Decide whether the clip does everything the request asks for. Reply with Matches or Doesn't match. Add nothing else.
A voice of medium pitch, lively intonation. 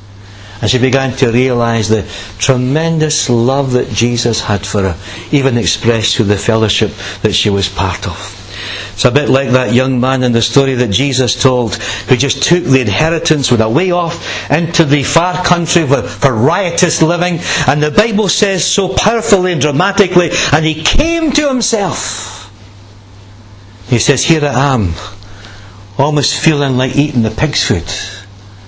Doesn't match